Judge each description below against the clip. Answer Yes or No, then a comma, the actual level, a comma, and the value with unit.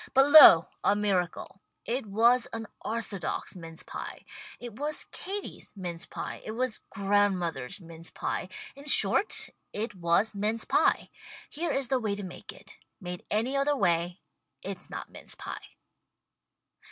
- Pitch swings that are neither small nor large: No, wide, 5.7 semitones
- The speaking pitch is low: No, high, 210 Hz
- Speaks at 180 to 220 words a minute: No, average, 150 wpm